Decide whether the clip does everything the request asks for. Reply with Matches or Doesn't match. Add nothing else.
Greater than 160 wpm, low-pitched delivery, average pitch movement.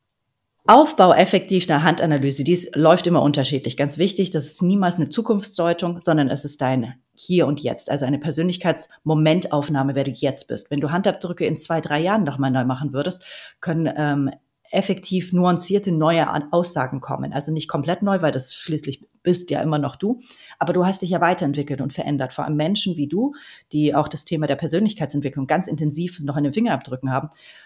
Doesn't match